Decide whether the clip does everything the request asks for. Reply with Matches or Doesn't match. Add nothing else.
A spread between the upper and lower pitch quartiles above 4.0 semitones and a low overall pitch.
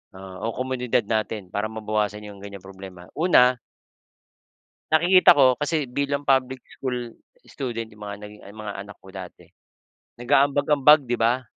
Matches